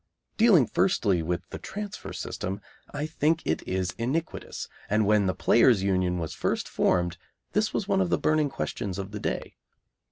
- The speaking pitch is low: Yes, low, 105 Hz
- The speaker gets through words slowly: No, average, 170 wpm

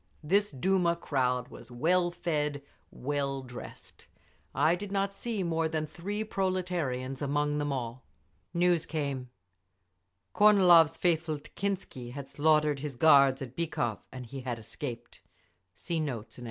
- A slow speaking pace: Yes, slow, 125 wpm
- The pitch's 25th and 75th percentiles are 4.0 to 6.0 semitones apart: Yes, average, 4.9 semitones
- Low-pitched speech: No, medium, 150 Hz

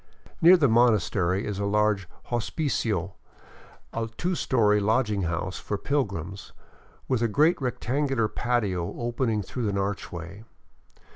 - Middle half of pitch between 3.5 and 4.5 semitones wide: Yes, average, 4.0 semitones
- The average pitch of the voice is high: No, low, 110 Hz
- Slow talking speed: Yes, slow, 125 wpm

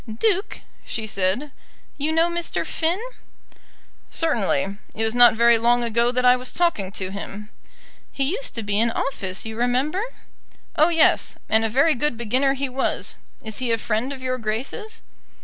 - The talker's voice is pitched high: Yes, high, 245 Hz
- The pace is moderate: Yes, average, 170 wpm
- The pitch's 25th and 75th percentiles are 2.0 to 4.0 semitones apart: No, average, 5.1 semitones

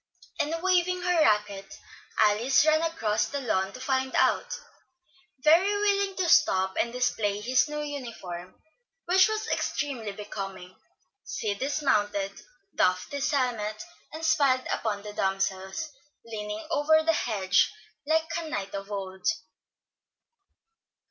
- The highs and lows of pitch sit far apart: Yes, wide, 7.6 semitones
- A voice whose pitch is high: Yes, high, 245 Hz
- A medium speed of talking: No, slow, 125 wpm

